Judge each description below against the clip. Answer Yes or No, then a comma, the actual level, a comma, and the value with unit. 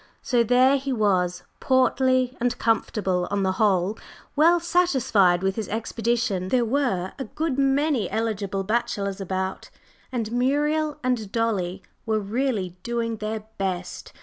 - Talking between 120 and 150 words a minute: Yes, average, 140 wpm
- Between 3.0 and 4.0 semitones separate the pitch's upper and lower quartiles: No, average, 5.0 semitones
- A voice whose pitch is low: No, high, 225 Hz